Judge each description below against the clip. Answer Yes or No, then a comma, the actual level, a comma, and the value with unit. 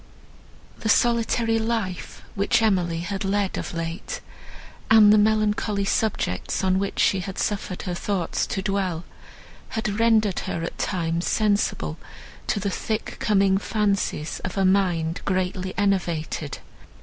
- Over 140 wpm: No, slow, 135 wpm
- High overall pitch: Yes, high, 195 Hz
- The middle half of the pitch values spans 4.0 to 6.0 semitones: No, average, 2.8 semitones